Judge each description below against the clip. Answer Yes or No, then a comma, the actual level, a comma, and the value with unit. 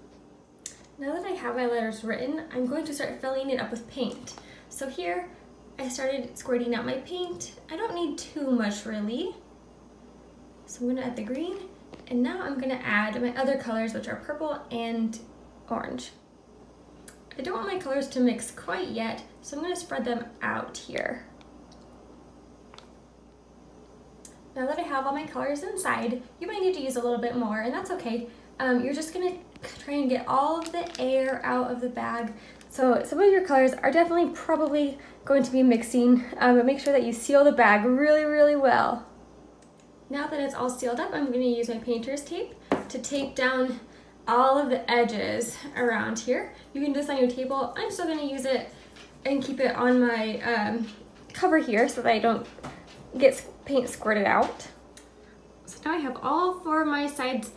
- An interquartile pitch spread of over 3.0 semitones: Yes, average, 3.4 semitones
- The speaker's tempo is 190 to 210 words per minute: Yes, average, 195 wpm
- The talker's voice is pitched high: Yes, very high, 260 Hz